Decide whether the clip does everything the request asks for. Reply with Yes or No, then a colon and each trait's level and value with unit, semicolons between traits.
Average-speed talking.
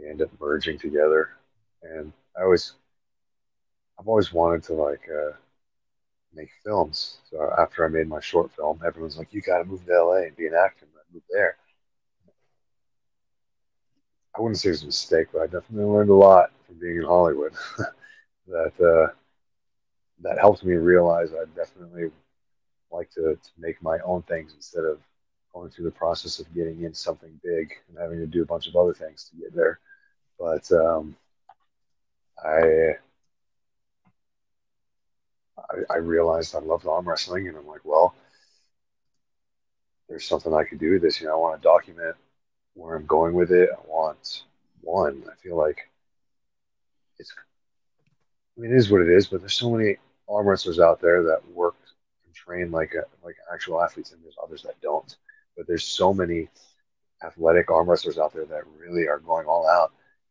Yes: average, 170 wpm